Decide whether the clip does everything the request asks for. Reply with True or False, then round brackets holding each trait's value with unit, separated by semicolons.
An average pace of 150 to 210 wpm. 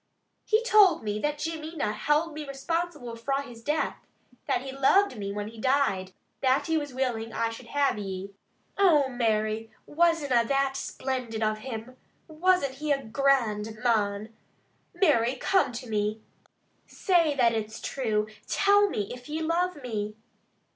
True (155 wpm)